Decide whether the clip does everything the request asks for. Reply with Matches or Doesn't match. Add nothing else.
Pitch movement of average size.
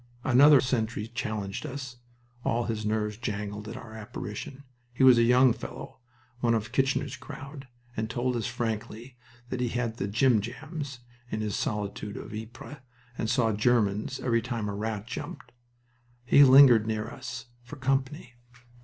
Matches